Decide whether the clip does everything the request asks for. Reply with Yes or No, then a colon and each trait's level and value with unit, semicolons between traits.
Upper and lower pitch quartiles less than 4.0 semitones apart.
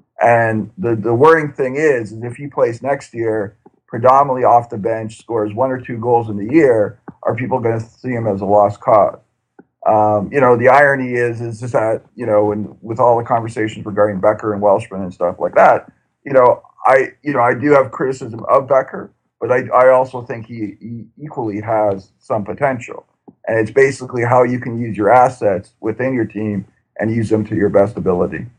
Yes: average, 3.0 semitones